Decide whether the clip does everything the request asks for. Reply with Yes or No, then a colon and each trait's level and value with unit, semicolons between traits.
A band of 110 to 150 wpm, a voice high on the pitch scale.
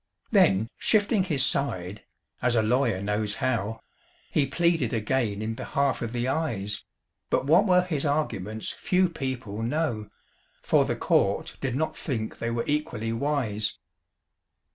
No: average, 140 wpm; low, 125 Hz